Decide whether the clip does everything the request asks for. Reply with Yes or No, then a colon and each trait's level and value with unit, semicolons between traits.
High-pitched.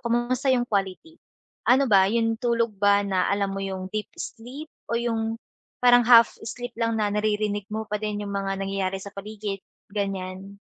Yes: high, 210 Hz